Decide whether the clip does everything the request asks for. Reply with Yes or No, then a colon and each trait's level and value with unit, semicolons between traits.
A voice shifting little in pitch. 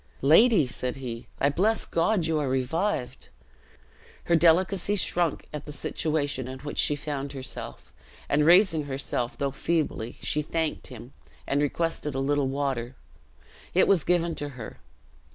No: average, 3.7 semitones